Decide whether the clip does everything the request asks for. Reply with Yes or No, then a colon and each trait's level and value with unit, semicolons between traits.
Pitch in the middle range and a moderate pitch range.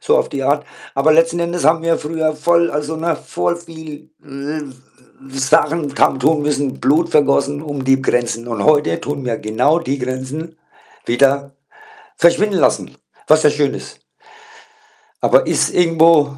Yes: medium, 150 Hz; average, 3.0 semitones